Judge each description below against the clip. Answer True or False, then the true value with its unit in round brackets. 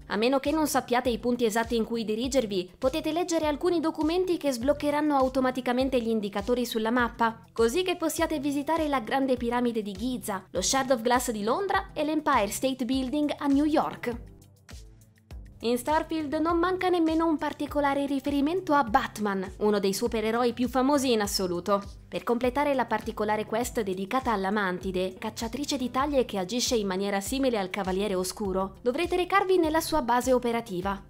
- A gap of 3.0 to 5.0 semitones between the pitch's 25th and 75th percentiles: False (5.4 semitones)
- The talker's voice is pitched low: False (250 Hz)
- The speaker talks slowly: False (165 wpm)